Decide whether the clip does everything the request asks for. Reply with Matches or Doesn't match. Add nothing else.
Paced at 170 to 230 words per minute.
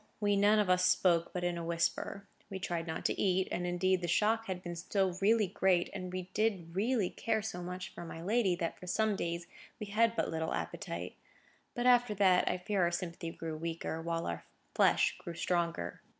Matches